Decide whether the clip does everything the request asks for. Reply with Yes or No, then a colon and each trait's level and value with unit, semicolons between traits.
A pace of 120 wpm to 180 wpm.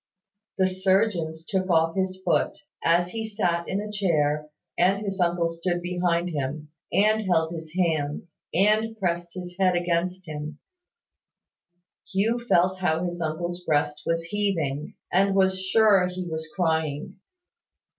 Yes: average, 140 wpm